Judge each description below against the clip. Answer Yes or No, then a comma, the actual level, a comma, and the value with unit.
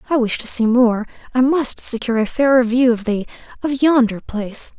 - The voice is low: No, high, 240 Hz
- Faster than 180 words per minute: No, average, 175 wpm